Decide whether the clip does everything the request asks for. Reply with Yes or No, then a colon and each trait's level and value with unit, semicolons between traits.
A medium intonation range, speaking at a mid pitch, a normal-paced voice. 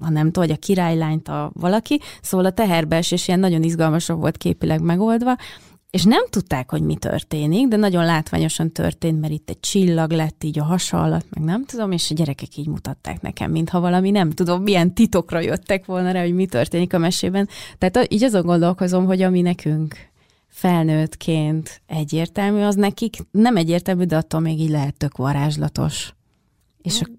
No: average, 3.1 semitones; medium, 170 Hz; fast, 180 wpm